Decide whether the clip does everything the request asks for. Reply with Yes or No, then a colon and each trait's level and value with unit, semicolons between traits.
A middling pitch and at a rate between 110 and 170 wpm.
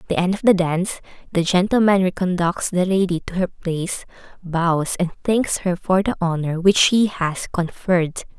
No: medium, 180 Hz; average, 185 wpm